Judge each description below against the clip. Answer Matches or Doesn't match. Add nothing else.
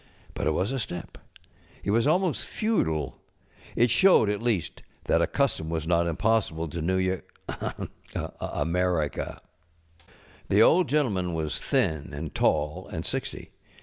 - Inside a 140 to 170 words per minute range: Matches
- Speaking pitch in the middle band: Doesn't match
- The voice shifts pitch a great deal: Matches